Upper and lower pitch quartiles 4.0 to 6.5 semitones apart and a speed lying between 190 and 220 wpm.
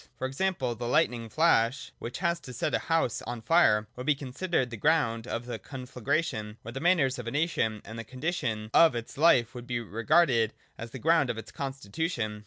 Yes: average, 5.3 semitones; average, 200 wpm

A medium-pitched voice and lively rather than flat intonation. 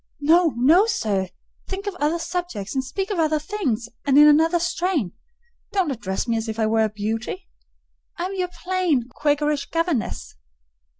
No: very high, 300 Hz; wide, 7.5 semitones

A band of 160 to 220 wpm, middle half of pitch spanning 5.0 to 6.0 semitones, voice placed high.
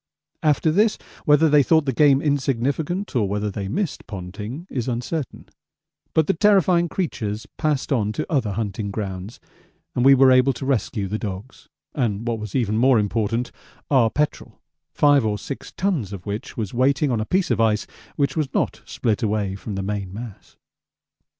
No: average, 175 wpm; wide, 5.6 semitones; low, 120 Hz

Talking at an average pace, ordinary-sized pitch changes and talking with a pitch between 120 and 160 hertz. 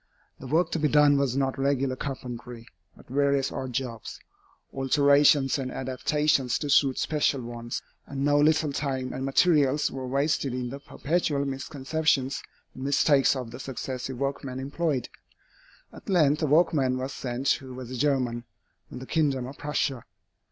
No: average, 160 wpm; narrow, 2.1 semitones; low, 135 Hz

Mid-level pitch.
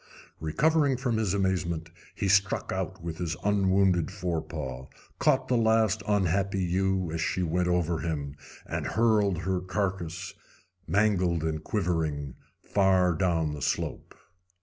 No: very low, 90 Hz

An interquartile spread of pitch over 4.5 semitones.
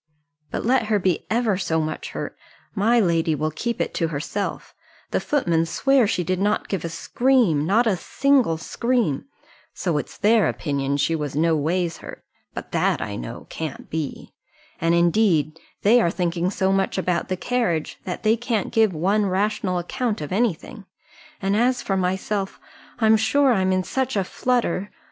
Yes: average, 5.1 semitones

